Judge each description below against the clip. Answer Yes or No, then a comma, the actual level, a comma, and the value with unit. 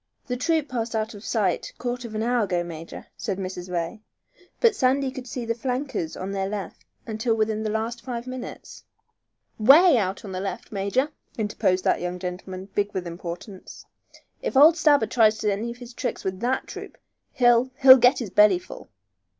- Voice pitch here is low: No, high, 220 Hz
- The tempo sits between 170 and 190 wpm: Yes, average, 185 wpm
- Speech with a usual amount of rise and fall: Yes, average, 4.6 semitones